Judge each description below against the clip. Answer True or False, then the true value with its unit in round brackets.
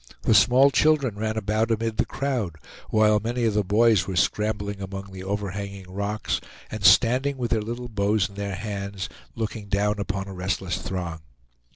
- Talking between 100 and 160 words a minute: False (175 wpm)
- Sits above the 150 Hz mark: False (105 Hz)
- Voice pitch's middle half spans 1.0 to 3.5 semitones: True (2.5 semitones)